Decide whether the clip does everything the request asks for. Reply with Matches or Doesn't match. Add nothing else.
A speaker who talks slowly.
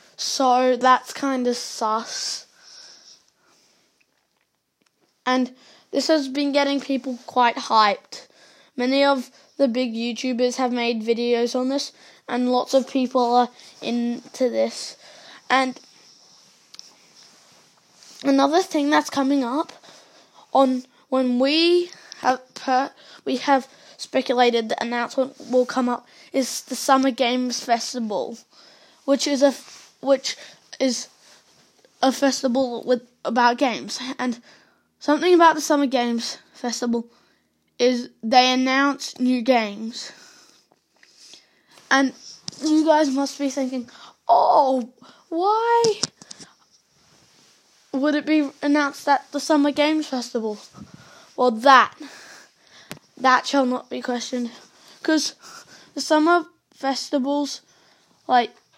Matches